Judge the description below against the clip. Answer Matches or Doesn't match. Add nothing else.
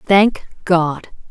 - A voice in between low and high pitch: Matches